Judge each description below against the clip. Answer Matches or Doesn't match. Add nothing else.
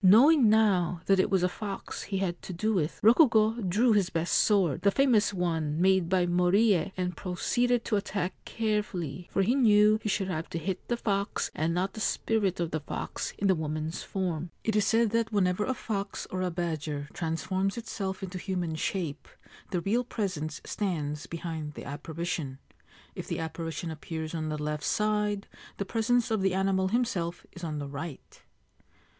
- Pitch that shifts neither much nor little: Matches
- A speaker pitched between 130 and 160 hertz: Doesn't match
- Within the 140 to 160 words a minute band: Doesn't match